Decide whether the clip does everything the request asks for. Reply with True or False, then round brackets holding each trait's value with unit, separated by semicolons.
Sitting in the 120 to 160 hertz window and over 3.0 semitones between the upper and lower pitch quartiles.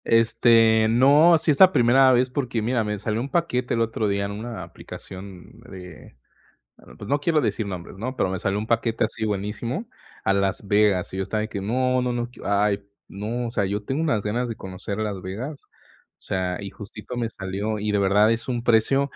False (110 Hz; 3.6 semitones)